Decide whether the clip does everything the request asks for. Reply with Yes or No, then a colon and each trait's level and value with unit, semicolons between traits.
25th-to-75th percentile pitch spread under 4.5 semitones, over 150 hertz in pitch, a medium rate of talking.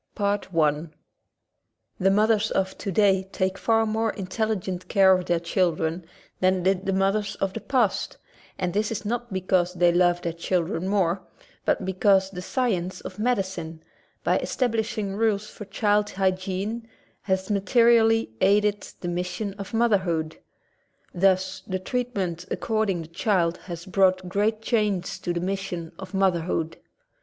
Yes: narrow, 2.6 semitones; high, 190 Hz; average, 150 wpm